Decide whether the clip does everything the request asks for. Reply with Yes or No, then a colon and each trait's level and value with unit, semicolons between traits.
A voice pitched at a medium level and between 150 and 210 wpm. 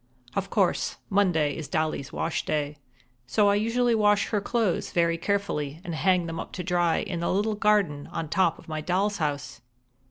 Yes: medium, 175 Hz; average, 185 wpm